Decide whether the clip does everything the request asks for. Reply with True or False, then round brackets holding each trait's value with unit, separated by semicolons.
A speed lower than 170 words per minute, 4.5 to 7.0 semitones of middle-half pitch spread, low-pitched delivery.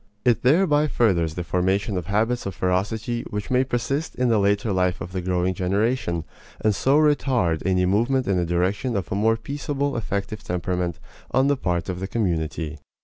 False (185 wpm; 5.3 semitones; 100 Hz)